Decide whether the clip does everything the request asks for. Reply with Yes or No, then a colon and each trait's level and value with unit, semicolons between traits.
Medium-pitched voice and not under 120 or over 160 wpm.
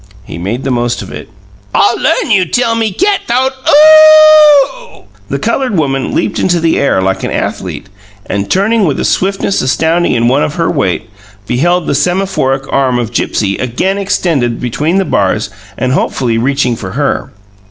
No: medium, 160 Hz; average, 175 wpm